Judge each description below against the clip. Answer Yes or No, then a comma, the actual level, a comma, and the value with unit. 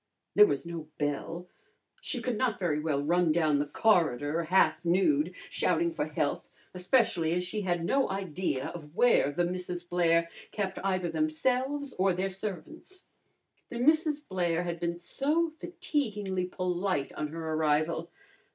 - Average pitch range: No, wide, 6.4 semitones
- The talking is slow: No, average, 150 wpm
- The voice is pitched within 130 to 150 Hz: No, medium, 180 Hz